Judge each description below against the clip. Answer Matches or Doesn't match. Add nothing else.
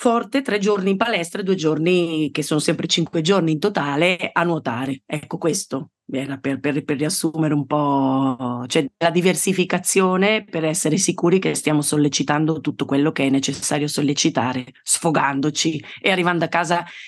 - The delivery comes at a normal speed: Matches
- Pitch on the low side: Doesn't match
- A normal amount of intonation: Matches